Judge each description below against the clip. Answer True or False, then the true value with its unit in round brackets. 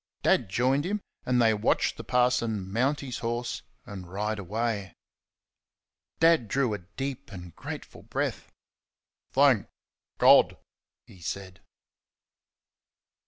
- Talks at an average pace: False (115 wpm)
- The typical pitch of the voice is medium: False (115 Hz)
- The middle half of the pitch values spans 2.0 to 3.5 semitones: False (4.4 semitones)